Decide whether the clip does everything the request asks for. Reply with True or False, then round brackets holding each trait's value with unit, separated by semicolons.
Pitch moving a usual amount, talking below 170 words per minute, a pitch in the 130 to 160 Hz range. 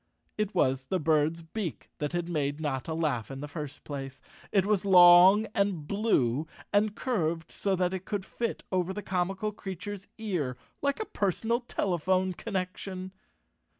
False (4.4 semitones; 155 wpm; 185 Hz)